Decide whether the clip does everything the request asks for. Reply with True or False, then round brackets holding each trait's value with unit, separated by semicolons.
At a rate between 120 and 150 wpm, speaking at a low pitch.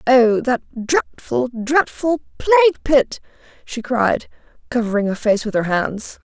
False (135 wpm; 250 Hz)